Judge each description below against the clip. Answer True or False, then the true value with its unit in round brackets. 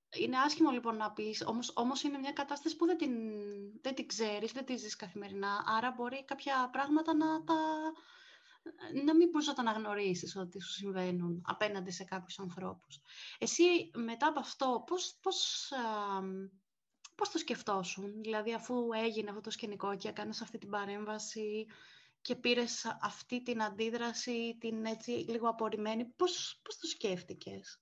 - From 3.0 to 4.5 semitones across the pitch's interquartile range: False (5.2 semitones)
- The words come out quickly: False (155 wpm)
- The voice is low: False (230 Hz)